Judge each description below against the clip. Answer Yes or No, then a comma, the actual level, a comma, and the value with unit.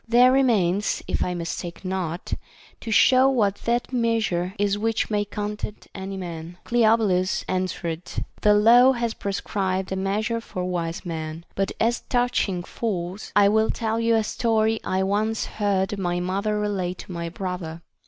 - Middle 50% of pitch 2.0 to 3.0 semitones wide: No, average, 3.6 semitones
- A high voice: Yes, high, 200 Hz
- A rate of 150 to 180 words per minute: Yes, average, 160 wpm